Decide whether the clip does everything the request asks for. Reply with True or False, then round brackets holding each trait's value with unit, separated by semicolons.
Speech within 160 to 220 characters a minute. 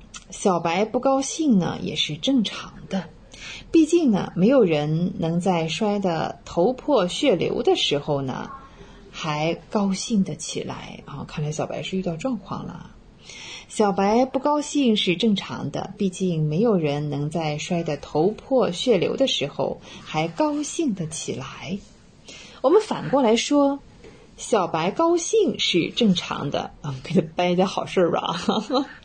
True (210 characters per minute)